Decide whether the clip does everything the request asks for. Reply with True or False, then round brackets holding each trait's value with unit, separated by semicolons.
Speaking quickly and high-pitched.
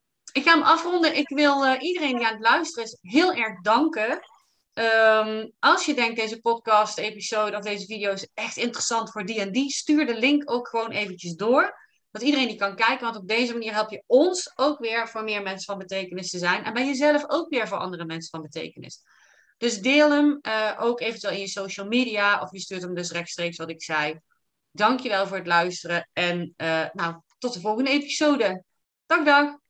True (205 wpm; 225 Hz)